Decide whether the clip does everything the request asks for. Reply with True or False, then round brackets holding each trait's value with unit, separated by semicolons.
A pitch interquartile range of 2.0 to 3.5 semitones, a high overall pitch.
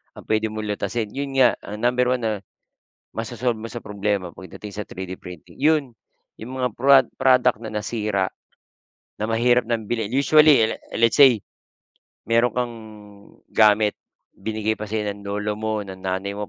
False (2.9 semitones; 110 Hz)